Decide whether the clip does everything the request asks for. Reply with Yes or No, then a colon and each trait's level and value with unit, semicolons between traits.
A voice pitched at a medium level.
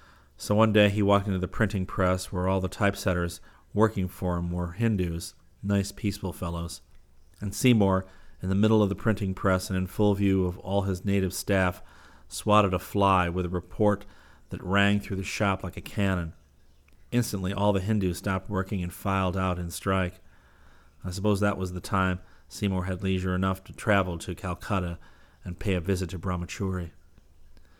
No: very low, 95 Hz